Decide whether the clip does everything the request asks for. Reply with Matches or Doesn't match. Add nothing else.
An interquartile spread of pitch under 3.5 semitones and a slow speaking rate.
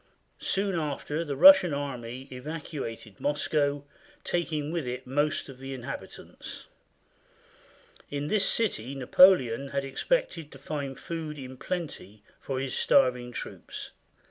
Doesn't match